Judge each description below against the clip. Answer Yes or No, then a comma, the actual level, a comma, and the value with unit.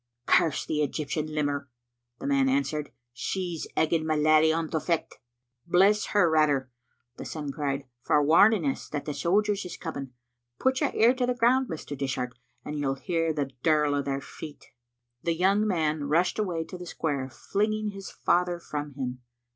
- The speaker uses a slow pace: No, average, 175 wpm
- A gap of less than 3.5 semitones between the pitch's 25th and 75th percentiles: No, average, 4.9 semitones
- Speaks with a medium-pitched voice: Yes, medium, 160 Hz